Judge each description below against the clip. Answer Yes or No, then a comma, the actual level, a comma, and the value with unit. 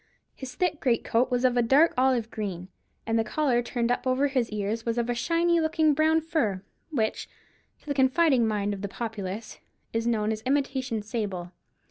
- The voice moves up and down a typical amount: Yes, average, 4.2 semitones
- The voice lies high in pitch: Yes, high, 240 Hz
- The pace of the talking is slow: No, average, 185 wpm